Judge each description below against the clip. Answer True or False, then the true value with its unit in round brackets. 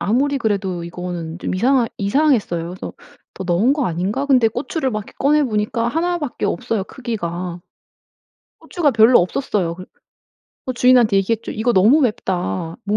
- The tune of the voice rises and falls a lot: True (6.0 semitones)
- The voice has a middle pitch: False (215 Hz)